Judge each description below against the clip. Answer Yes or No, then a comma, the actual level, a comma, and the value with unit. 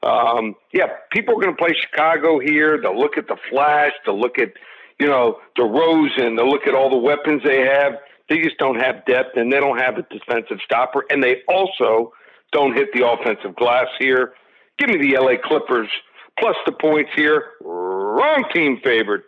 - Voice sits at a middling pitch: Yes, medium, 145 Hz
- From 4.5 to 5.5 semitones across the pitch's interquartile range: No, average, 3.3 semitones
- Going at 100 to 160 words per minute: No, average, 195 wpm